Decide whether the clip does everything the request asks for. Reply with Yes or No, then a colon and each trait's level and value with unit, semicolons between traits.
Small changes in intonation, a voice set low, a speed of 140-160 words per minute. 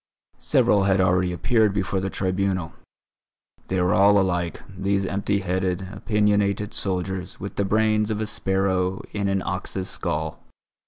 Yes: narrow, 1.6 semitones; very low, 95 Hz; average, 145 wpm